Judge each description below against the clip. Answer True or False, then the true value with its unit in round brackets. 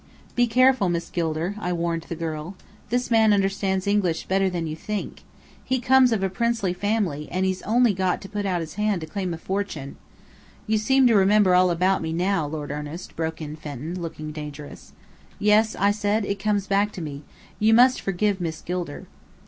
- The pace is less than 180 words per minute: False (195 wpm)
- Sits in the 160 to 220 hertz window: True (190 Hz)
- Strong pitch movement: False (4.1 semitones)